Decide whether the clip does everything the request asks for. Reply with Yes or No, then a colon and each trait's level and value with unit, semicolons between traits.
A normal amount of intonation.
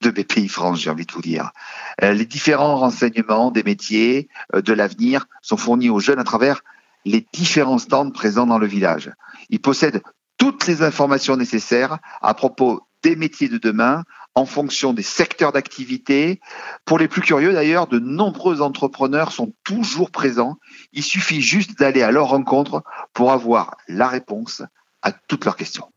No: wide, 6.5 semitones